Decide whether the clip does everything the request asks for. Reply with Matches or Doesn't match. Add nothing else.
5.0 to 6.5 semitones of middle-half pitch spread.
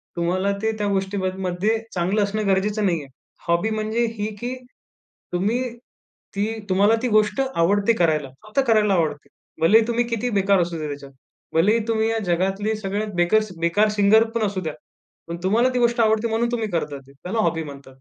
Doesn't match